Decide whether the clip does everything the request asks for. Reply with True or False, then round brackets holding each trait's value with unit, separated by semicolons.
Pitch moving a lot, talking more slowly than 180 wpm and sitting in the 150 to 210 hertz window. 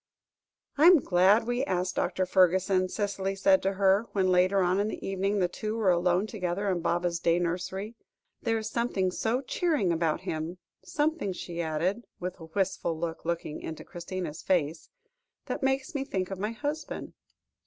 False (3.4 semitones; 170 wpm; 190 Hz)